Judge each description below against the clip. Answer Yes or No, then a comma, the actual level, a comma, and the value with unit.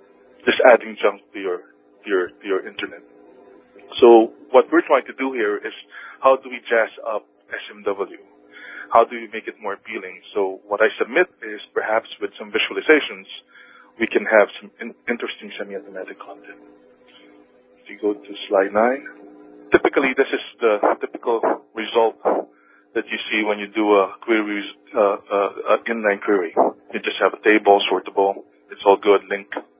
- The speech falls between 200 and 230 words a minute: No, average, 165 wpm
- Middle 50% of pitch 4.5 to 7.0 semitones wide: Yes, wide, 5.5 semitones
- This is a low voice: Yes, low, 105 Hz